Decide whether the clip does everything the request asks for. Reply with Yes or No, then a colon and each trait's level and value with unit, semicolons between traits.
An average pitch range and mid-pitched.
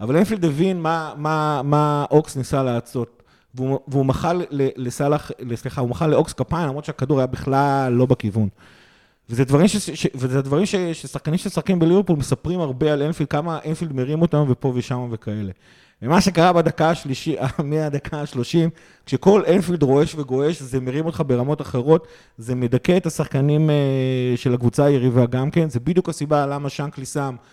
Yes: average, 3.8 semitones; medium, 145 Hz